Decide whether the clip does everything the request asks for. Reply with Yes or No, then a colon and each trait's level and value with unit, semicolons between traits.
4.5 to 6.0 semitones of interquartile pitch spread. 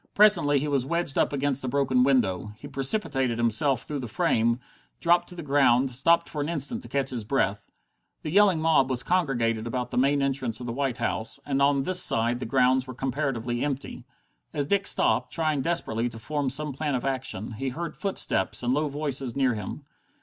No: average, 3.3 semitones